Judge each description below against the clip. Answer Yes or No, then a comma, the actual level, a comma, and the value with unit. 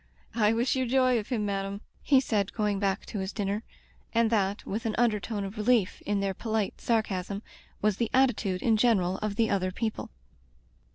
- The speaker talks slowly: No, average, 185 wpm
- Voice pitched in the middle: No, high, 210 Hz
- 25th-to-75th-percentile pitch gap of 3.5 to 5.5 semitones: No, narrow, 2.6 semitones